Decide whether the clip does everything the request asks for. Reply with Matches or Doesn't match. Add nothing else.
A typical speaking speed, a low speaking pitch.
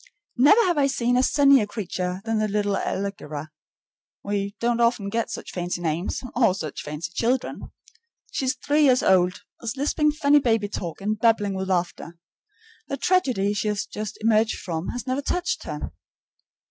Doesn't match